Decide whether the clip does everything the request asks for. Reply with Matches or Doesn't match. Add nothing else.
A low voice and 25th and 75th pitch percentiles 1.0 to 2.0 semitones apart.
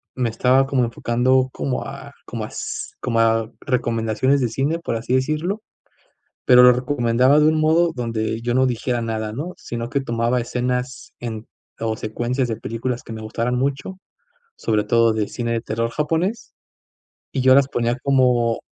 Doesn't match